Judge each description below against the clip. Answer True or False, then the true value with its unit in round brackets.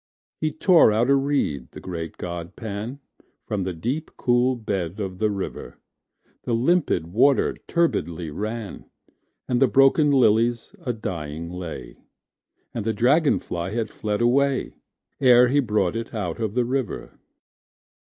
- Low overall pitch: True (115 Hz)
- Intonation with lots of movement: True (6.0 semitones)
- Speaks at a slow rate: True (130 wpm)